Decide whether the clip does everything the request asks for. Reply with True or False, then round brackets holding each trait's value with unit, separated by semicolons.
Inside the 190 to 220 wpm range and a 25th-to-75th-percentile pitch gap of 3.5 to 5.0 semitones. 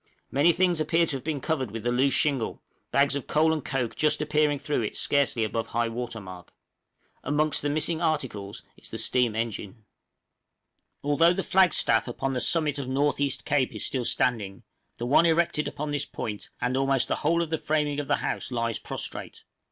True (200 wpm; 4.3 semitones)